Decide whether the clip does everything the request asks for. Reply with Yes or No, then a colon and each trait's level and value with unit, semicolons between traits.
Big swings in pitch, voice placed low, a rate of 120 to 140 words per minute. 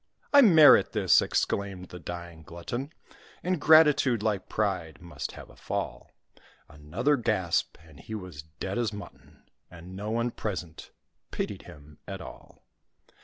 Yes: wide, 5.8 semitones; very low, 95 Hz; slow, 135 wpm